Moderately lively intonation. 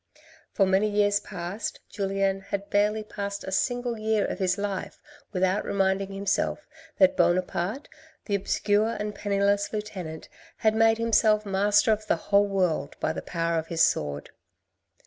No: narrow, 1.9 semitones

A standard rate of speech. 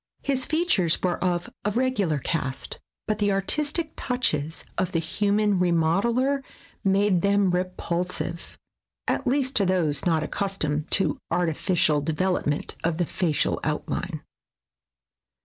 No: slow, 125 wpm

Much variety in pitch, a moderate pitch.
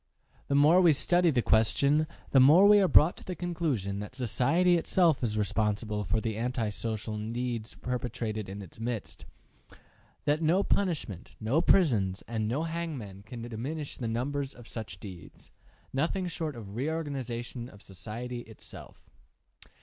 No: wide, 6.2 semitones; low, 125 Hz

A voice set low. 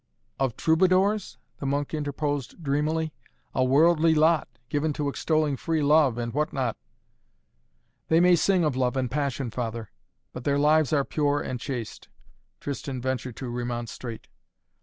No: medium, 145 Hz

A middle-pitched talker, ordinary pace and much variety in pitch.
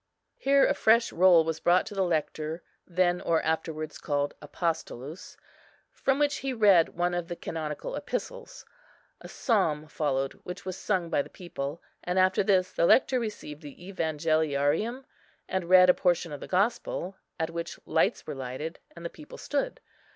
No: medium, 175 Hz; average, 165 wpm; average, 3.5 semitones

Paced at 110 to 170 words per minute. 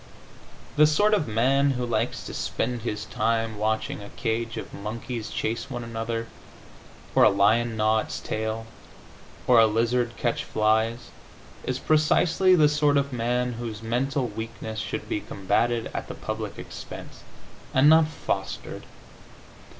Yes: average, 145 wpm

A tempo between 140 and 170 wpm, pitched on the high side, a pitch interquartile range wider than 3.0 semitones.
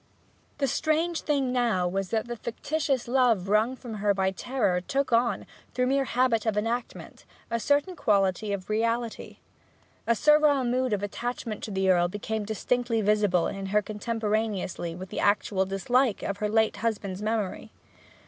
Yes: average, 160 wpm; high, 220 Hz; average, 3.7 semitones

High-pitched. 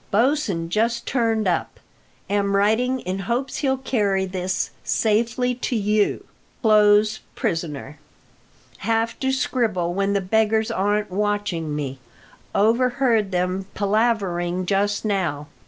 Yes: high, 205 Hz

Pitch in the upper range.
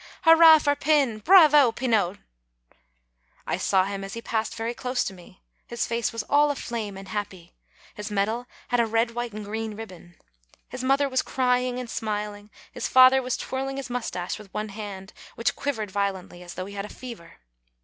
Yes: high, 225 Hz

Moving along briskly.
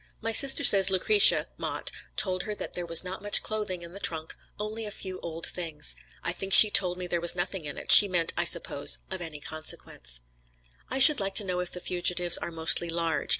Yes: fast, 220 wpm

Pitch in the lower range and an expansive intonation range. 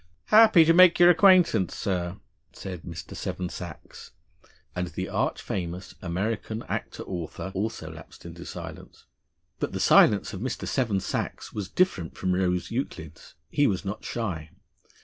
Yes: very low, 95 Hz; wide, 5.9 semitones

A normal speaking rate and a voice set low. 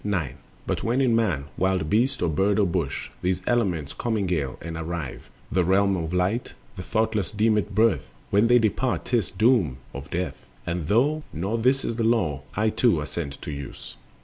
Yes: average, 180 wpm; very low, 95 Hz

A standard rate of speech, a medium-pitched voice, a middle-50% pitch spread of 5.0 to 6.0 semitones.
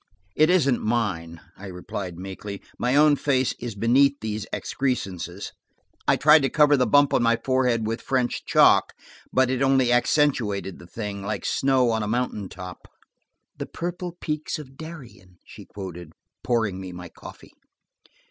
No: average, 155 wpm; low, 120 Hz; wide, 5.6 semitones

